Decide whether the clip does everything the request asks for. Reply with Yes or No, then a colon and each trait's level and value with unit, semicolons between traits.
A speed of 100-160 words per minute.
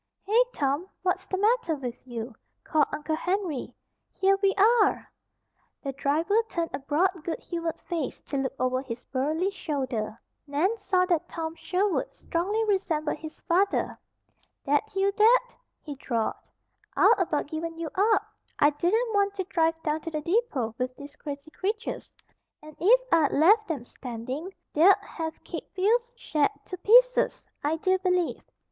Yes: average, 155 wpm